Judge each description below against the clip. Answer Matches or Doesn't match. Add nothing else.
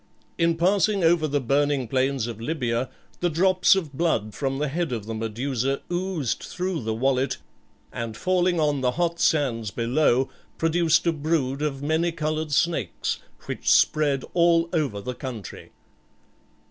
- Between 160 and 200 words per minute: Doesn't match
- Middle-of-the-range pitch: Matches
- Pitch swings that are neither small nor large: Matches